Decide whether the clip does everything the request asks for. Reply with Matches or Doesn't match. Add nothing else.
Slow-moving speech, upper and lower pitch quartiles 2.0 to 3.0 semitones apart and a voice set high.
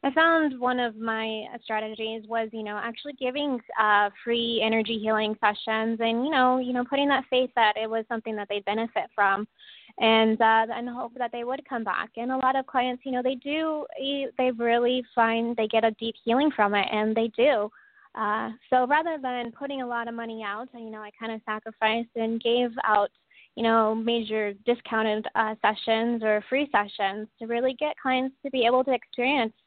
Doesn't match